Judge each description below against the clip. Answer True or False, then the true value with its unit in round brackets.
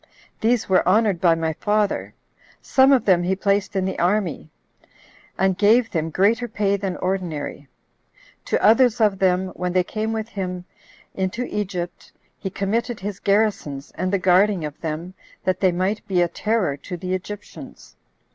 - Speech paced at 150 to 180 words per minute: True (165 wpm)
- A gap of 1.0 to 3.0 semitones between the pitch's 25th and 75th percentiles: True (2.7 semitones)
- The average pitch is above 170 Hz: True (190 Hz)